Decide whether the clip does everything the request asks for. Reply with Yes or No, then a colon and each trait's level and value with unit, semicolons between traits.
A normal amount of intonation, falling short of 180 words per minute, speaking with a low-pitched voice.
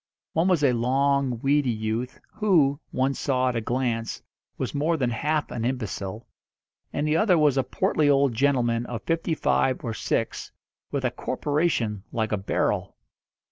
Yes: average, 3.8 semitones; average, 165 wpm; low, 130 Hz